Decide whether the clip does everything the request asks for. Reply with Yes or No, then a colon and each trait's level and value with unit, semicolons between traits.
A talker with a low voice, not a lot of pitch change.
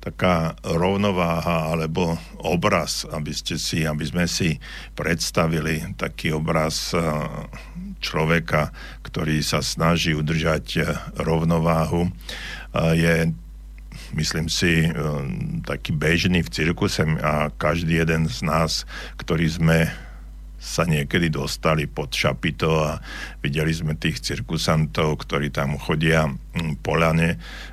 Yes: very low, 80 Hz; narrow, 1.2 semitones